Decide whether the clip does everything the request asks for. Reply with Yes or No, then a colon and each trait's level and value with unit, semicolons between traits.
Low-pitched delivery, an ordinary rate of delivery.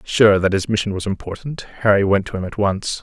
No: low, 100 Hz; fast, 240 wpm